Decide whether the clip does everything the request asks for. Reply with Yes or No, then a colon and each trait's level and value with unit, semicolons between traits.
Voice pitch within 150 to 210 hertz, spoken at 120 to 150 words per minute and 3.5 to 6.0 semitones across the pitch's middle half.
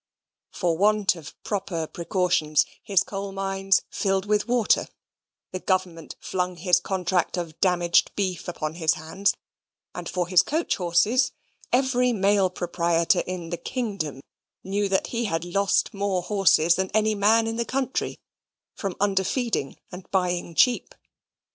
No: high, 190 Hz; average, 140 wpm; average, 2.9 semitones